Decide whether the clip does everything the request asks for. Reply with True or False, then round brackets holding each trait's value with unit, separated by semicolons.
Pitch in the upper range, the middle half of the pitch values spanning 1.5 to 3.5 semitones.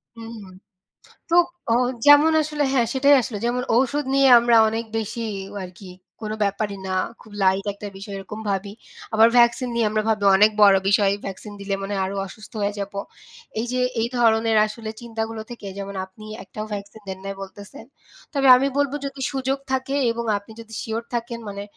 True (220 Hz; 3.1 semitones)